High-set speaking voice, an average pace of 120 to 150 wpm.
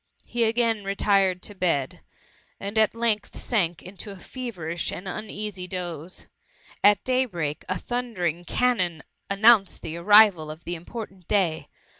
Yes: high, 195 Hz; average, 140 wpm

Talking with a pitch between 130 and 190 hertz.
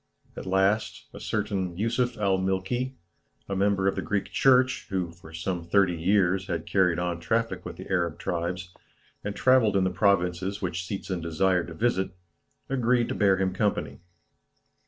No: very low, 95 Hz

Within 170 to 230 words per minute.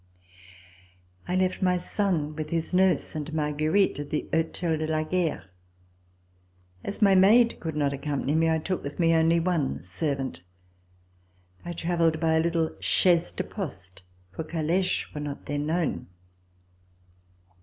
No: average, 145 wpm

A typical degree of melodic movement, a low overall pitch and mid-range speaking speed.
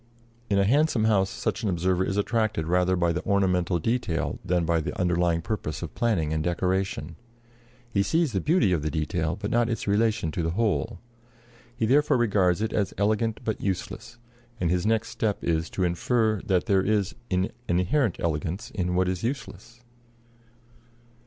Yes: average, 4.2 semitones; very low, 95 Hz; average, 175 wpm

